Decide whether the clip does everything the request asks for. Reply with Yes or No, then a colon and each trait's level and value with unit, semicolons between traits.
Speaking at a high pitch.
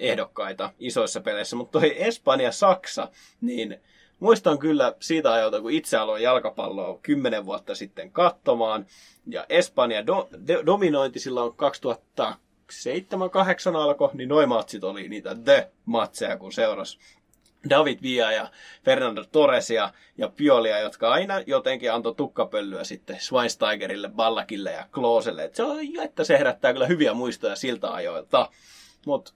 Yes: very high, 260 Hz